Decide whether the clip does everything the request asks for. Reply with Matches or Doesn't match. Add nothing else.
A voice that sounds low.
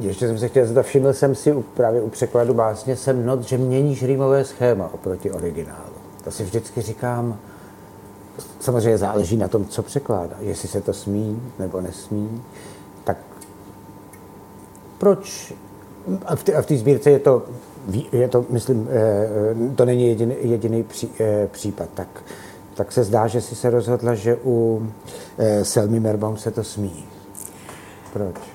Matches